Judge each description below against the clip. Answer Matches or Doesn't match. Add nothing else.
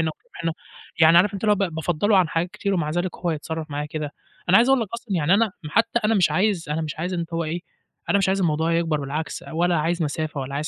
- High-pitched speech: Doesn't match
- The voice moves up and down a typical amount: Matches